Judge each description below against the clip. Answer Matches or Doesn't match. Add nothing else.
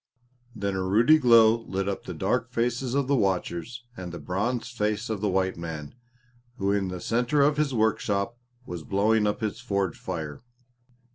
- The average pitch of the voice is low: Matches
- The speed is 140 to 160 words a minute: Doesn't match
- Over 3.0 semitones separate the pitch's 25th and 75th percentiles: Matches